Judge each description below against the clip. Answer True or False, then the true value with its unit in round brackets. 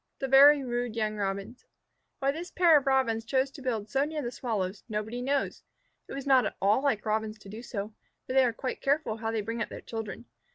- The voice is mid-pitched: False (240 Hz)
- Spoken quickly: True (230 wpm)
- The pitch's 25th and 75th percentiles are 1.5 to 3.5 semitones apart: False (4.0 semitones)